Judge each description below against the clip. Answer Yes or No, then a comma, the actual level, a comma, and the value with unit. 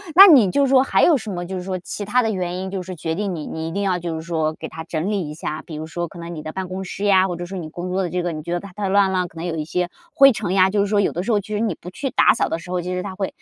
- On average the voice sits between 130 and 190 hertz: Yes, medium, 185 Hz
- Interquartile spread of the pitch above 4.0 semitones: No, average, 2.9 semitones